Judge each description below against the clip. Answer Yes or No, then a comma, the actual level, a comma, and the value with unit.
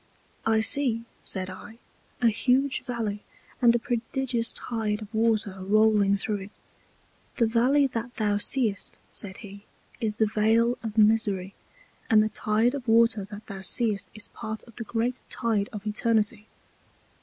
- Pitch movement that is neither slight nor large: No, narrow, 2.1 semitones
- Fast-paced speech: No, average, 155 wpm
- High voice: Yes, high, 220 Hz